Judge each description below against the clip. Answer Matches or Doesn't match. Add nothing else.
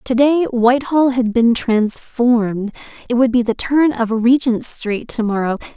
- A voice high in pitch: Matches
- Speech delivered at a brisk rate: Doesn't match